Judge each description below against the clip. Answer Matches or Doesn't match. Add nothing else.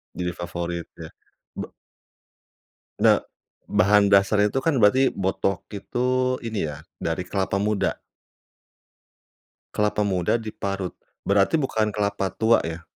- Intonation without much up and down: Doesn't match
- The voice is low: Matches